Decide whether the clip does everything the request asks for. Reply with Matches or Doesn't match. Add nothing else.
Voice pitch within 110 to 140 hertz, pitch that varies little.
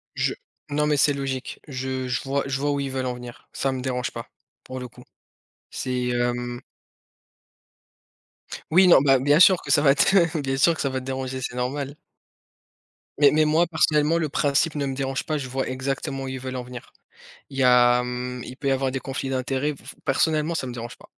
Matches